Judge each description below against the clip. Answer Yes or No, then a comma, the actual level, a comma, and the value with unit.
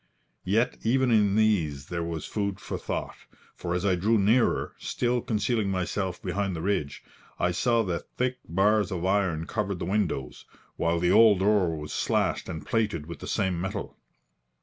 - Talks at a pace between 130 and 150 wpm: No, average, 170 wpm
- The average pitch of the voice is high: No, very low, 95 Hz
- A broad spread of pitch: No, average, 3.7 semitones